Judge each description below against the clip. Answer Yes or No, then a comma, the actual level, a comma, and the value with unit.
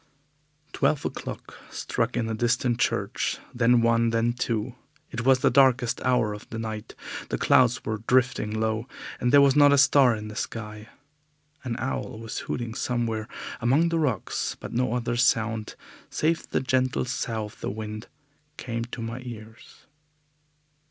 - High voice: No, low, 120 Hz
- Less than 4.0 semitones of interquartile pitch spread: Yes, narrow, 2.4 semitones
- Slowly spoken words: No, average, 160 wpm